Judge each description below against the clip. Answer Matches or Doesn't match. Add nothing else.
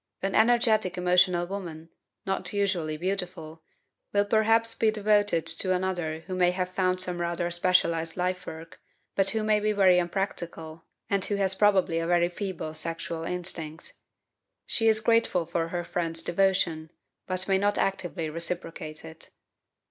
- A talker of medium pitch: Matches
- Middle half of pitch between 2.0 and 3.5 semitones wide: Matches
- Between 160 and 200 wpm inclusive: Doesn't match